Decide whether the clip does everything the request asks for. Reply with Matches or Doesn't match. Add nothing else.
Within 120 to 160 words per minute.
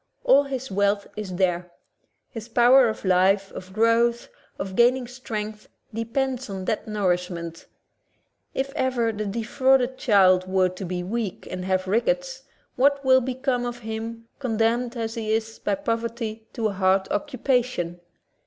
Matches